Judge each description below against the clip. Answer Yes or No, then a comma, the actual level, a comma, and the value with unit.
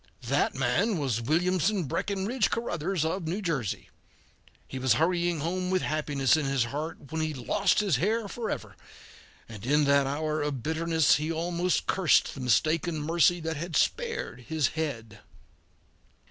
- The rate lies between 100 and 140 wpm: No, average, 150 wpm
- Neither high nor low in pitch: Yes, medium, 160 Hz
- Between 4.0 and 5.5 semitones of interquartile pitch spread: Yes, average, 4.3 semitones